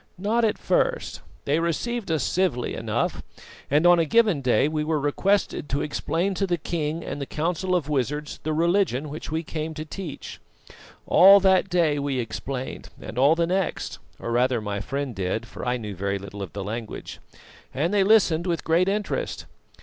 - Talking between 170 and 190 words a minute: Yes, average, 185 wpm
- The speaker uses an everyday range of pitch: No, wide, 5.7 semitones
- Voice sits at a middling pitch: Yes, medium, 155 Hz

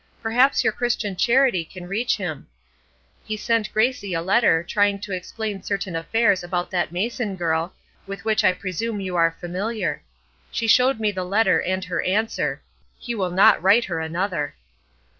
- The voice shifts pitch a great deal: No, average, 3.8 semitones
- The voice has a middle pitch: No, high, 195 Hz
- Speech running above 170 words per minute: No, average, 165 wpm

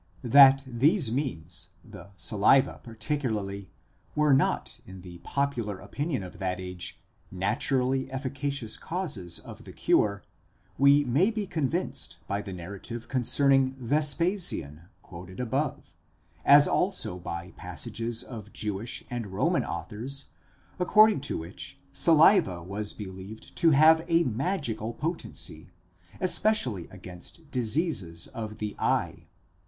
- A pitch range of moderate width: No, wide, 6.7 semitones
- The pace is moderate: No, slow, 115 wpm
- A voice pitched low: Yes, low, 120 Hz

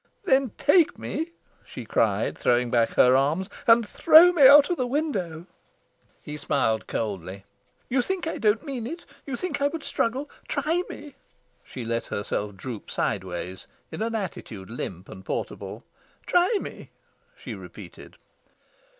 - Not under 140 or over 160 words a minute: Yes, average, 150 wpm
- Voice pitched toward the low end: No, high, 225 Hz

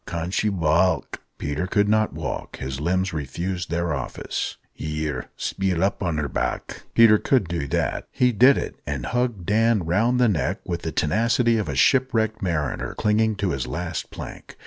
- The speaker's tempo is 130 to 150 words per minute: No, average, 170 wpm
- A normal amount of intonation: No, wide, 5.7 semitones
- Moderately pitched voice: No, very low, 90 Hz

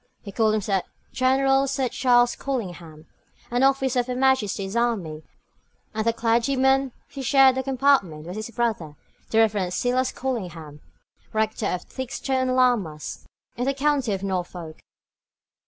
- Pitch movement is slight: No, average, 5.3 semitones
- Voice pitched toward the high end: Yes, high, 235 Hz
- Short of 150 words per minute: Yes, average, 140 wpm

